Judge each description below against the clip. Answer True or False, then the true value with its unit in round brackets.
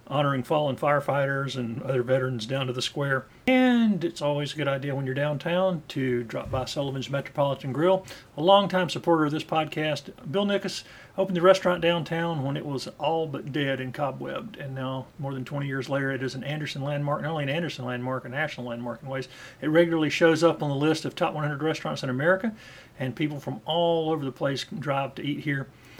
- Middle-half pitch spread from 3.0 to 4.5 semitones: True (3.6 semitones)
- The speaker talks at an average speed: False (210 wpm)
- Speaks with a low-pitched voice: False (145 Hz)